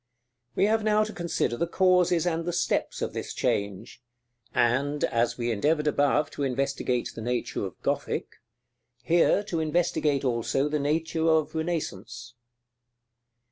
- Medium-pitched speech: Yes, medium, 150 Hz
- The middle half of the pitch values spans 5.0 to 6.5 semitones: Yes, wide, 5.5 semitones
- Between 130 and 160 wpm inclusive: Yes, average, 140 wpm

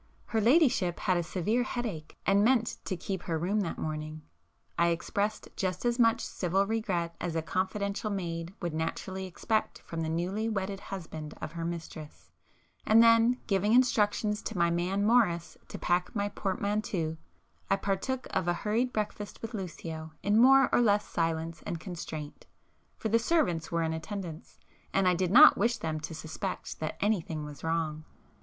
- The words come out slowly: No, average, 170 wpm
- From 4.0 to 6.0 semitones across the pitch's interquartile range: Yes, average, 4.5 semitones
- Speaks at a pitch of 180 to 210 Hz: Yes, high, 190 Hz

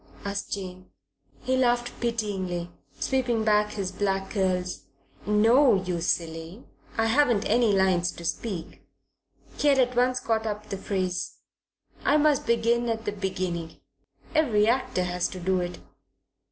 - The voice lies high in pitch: Yes, high, 210 Hz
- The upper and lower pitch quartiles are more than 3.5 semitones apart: Yes, average, 4.4 semitones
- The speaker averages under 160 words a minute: Yes, average, 140 wpm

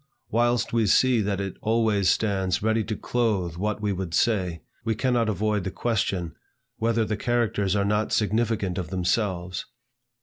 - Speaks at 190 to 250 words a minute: No, average, 160 wpm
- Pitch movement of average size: Yes, average, 3.1 semitones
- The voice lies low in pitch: Yes, low, 105 Hz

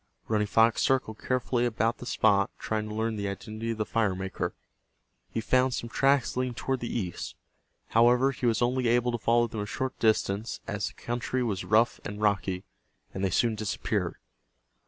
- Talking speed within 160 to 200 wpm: Yes, average, 180 wpm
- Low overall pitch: Yes, low, 115 Hz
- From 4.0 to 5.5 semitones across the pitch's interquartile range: No, narrow, 2.6 semitones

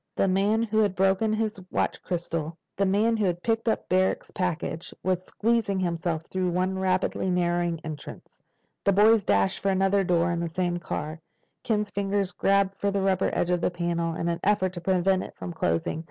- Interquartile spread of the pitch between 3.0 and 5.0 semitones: No, narrow, 2.6 semitones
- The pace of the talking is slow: No, average, 185 wpm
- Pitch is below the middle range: No, medium, 185 Hz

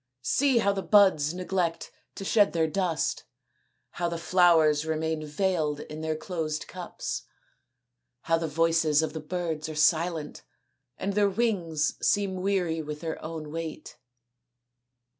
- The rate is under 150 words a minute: Yes, average, 140 wpm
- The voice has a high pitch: No, medium, 165 Hz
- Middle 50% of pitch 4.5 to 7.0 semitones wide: No, average, 3.1 semitones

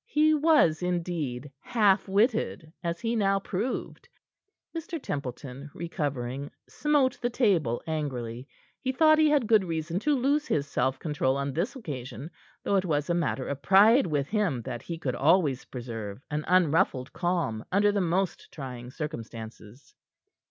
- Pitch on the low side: No, medium, 165 Hz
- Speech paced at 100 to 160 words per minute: Yes, average, 150 wpm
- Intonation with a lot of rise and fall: Yes, wide, 7.5 semitones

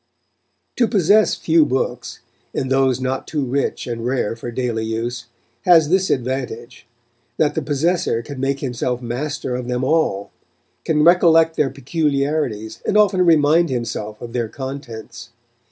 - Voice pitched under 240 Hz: Yes, low, 135 Hz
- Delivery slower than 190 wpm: Yes, average, 145 wpm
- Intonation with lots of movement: No, average, 4.7 semitones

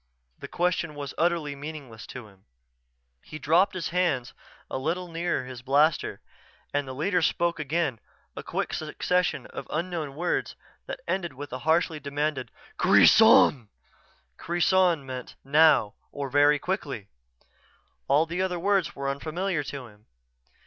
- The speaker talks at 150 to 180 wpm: No, average, 140 wpm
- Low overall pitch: No, medium, 150 Hz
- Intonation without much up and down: No, average, 4.1 semitones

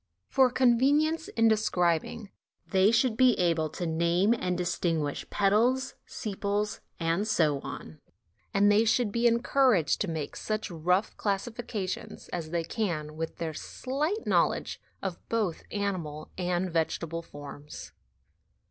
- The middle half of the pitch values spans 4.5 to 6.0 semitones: Yes, wide, 5.4 semitones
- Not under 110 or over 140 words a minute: Yes, slow, 135 wpm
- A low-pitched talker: No, high, 195 Hz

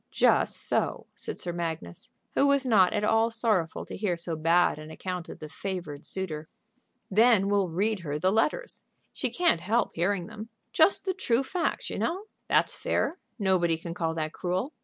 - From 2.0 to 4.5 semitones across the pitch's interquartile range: No, average, 5.1 semitones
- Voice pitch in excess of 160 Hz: Yes, high, 190 Hz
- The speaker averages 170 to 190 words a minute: Yes, average, 180 wpm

